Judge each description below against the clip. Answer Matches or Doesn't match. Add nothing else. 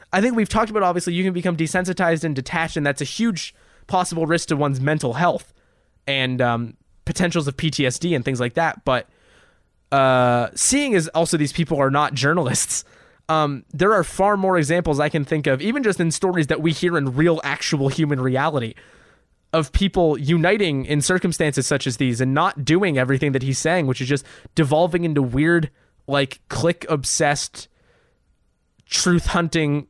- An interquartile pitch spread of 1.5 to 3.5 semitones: Doesn't match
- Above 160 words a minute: Matches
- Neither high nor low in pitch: Matches